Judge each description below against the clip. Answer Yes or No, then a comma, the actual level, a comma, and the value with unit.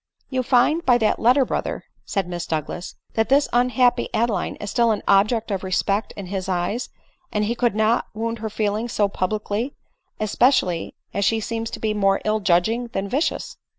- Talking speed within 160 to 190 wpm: No, average, 200 wpm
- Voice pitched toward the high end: Yes, high, 215 Hz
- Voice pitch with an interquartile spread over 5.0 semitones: No, average, 3.4 semitones